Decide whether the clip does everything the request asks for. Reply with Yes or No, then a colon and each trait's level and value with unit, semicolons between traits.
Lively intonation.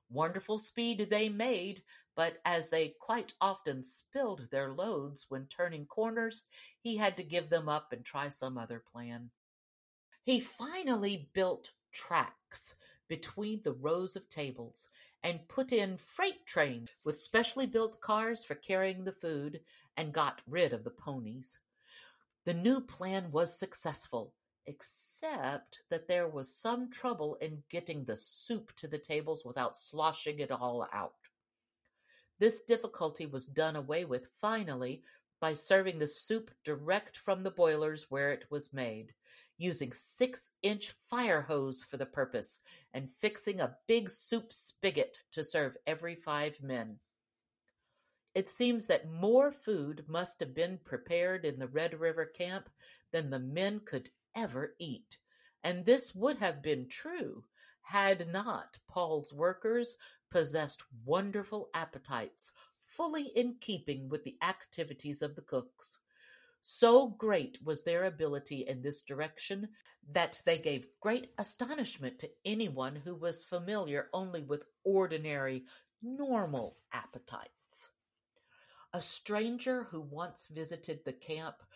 Yes: wide, 6.9 semitones